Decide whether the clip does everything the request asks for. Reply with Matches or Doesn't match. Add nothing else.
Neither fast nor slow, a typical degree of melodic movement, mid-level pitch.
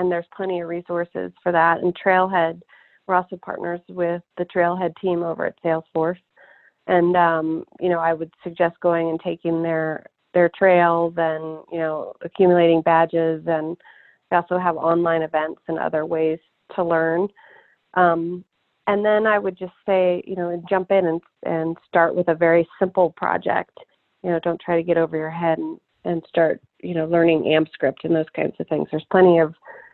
Doesn't match